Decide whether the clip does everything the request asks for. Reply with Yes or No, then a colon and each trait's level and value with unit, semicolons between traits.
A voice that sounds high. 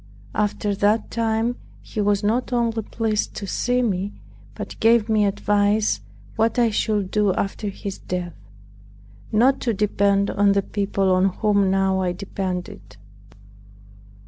Yes: high, 205 Hz